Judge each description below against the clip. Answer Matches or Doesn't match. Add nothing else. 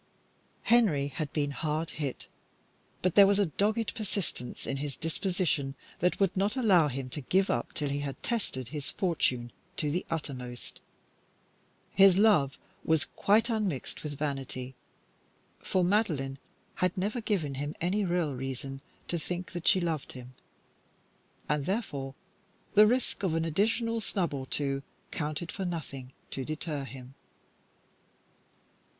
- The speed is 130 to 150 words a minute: Matches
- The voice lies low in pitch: Doesn't match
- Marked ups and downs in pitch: Matches